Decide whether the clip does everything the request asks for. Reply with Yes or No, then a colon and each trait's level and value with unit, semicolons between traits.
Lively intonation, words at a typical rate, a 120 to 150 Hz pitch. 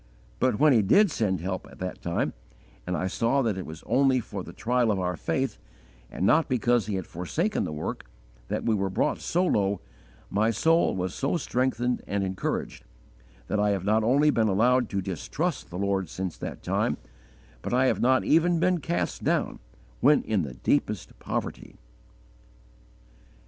No: wide, 5.8 semitones; average, 180 wpm; low, 110 Hz